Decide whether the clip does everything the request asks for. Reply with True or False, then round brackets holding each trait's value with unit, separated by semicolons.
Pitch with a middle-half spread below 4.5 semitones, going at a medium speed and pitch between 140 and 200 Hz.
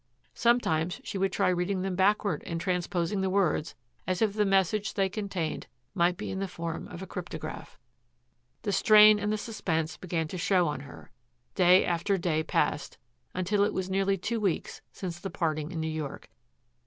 True (2.9 semitones; 180 wpm; 185 Hz)